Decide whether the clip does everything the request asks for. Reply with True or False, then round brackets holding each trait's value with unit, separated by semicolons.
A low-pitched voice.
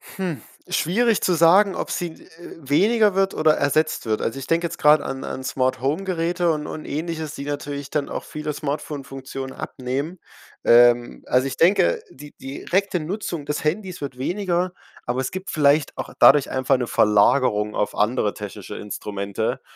False (145 Hz)